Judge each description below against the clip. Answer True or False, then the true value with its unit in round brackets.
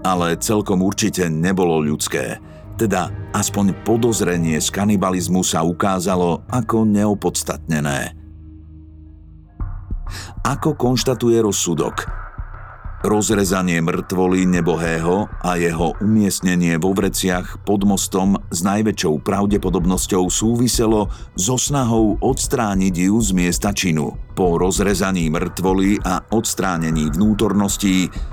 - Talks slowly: True (95 wpm)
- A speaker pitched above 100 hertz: False (95 Hz)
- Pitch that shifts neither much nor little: True (3.0 semitones)